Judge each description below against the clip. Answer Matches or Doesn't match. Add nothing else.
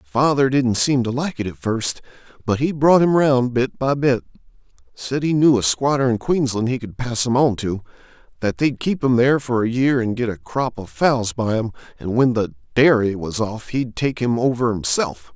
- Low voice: Matches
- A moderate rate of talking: Doesn't match